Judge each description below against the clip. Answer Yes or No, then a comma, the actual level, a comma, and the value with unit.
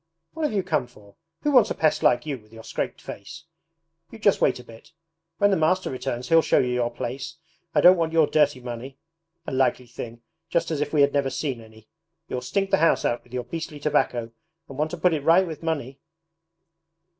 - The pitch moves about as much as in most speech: Yes, average, 4.9 semitones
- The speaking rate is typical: No, fast, 220 wpm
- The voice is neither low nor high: Yes, medium, 145 Hz